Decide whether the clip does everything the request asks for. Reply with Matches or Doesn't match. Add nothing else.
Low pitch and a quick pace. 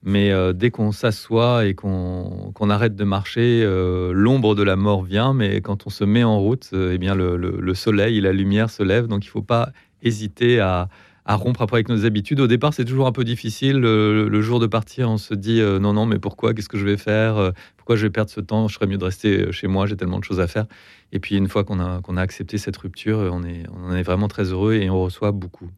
Matches